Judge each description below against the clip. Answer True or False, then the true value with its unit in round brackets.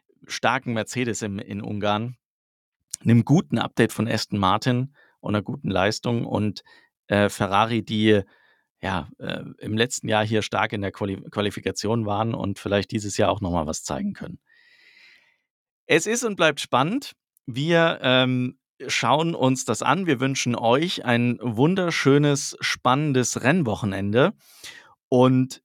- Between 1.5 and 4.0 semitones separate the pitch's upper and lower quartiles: False (4.7 semitones)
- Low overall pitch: True (115 Hz)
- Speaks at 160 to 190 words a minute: False (140 wpm)